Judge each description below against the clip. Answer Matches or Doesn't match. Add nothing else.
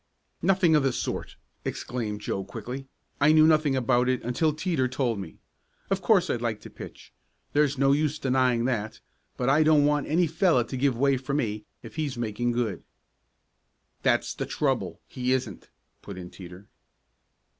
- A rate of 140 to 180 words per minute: Matches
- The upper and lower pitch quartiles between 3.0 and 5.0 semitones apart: Matches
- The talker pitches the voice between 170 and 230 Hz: Doesn't match